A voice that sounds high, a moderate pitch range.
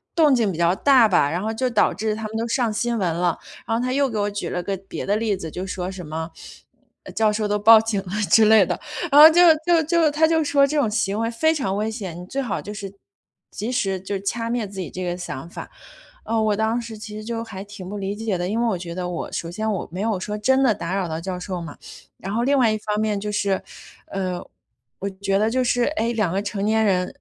Yes: high, 210 Hz; average, 3.4 semitones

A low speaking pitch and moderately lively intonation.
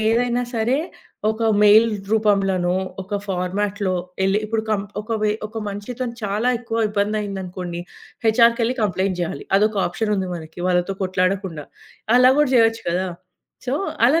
No: high, 210 Hz; average, 3.3 semitones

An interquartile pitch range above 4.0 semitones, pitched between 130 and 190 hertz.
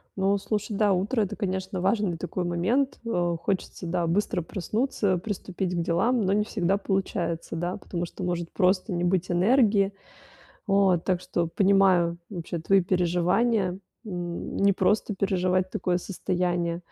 No: narrow, 2.4 semitones; medium, 185 Hz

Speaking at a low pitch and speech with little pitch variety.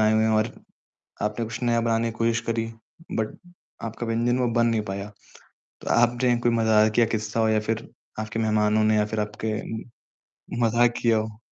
Yes: low, 110 Hz; narrow, 1.4 semitones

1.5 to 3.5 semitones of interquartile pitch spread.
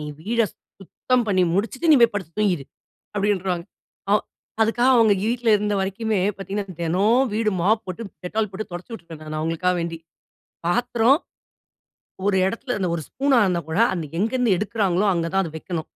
No: average, 4.4 semitones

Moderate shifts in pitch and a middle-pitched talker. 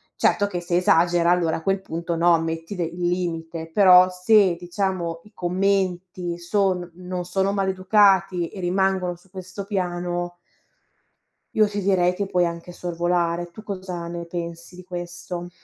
No: narrow, 1.7 semitones; medium, 180 Hz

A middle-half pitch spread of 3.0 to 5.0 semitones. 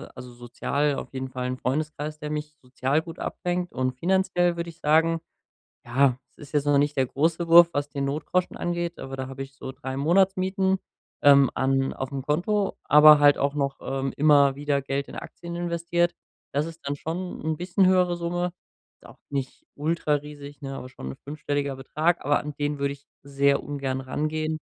Yes: average, 3.5 semitones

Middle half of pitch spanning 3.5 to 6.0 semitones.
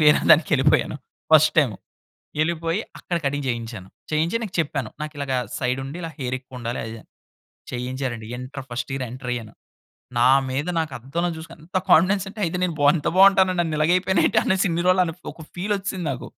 Yes: average, 5.1 semitones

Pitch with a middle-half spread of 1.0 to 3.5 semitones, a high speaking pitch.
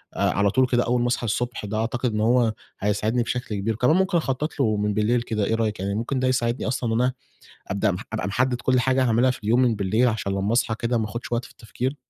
No: average, 2.8 semitones; low, 120 Hz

